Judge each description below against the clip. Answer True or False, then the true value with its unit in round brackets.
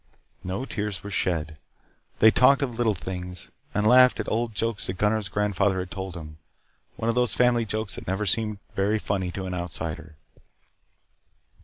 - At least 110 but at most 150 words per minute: False (170 wpm)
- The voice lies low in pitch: True (100 Hz)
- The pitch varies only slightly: False (3.5 semitones)